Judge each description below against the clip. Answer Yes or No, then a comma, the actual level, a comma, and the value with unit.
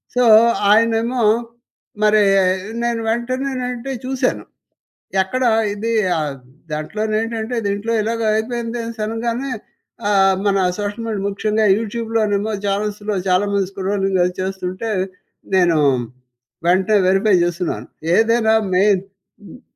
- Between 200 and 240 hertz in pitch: Yes, high, 210 Hz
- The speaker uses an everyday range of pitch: Yes, average, 3.0 semitones